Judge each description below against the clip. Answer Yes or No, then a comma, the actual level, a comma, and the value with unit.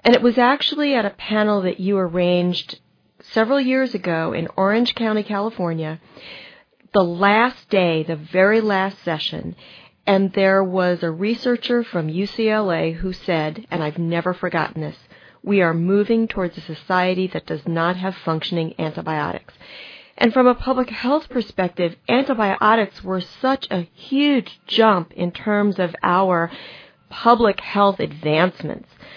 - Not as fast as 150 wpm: Yes, average, 140 wpm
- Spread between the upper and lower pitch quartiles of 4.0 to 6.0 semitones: Yes, average, 4.3 semitones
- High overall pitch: Yes, high, 195 Hz